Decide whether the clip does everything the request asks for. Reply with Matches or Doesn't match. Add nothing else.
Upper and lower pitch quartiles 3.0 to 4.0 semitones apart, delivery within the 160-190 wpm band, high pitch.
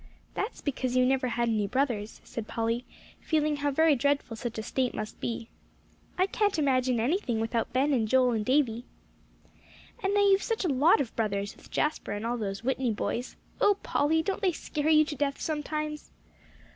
Doesn't match